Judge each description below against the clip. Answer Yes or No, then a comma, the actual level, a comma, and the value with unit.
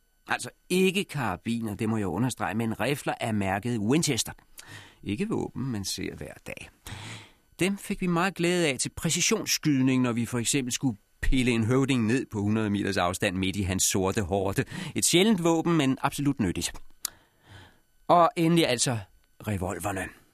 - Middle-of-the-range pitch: No, low, 120 Hz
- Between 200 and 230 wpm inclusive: No, average, 160 wpm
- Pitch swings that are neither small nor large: No, wide, 6.8 semitones